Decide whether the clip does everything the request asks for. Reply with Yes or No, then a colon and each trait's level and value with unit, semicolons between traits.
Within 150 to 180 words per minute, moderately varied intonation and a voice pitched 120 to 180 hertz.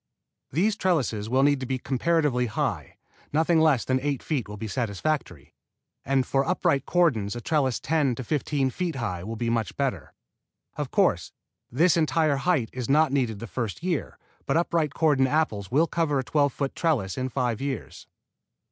Yes: average, 175 wpm; average, 4.7 semitones; low, 135 Hz